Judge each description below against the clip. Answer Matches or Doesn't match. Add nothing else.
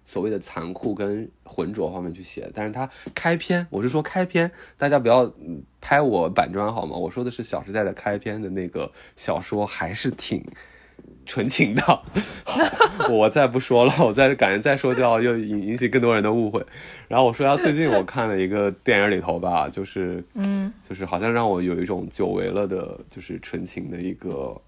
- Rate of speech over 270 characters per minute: Matches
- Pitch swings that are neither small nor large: Doesn't match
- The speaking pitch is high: Doesn't match